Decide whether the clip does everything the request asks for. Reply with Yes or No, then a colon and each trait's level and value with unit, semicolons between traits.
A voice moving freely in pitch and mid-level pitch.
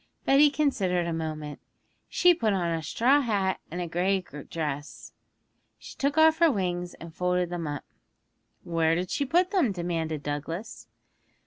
Yes: wide, 7.5 semitones; medium, 180 Hz